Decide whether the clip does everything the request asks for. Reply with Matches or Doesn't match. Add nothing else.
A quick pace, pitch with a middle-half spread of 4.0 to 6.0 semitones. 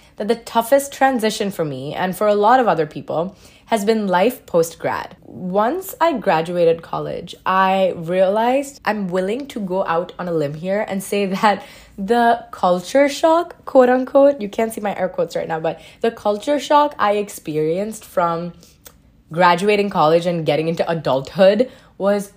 Doesn't match